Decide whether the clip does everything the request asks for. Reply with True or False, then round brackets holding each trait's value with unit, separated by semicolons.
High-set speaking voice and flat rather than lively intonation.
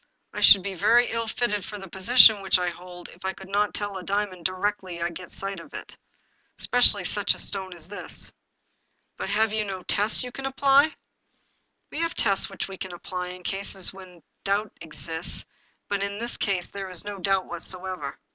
True (195 Hz; 2.2 semitones)